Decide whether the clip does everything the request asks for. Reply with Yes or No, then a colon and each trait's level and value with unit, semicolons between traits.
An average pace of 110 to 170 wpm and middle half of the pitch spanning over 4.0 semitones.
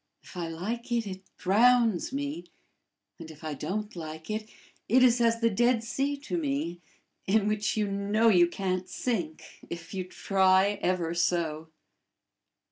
Yes: average, 155 wpm; average, 5.0 semitones